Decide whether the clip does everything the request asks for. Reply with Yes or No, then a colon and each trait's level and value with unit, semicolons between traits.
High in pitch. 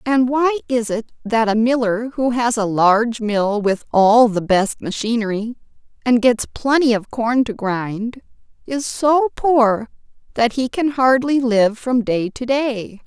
Yes: high, 235 Hz